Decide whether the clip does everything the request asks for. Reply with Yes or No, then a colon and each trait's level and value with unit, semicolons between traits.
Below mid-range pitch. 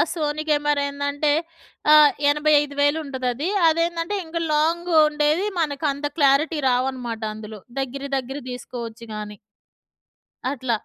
No: very high, 285 Hz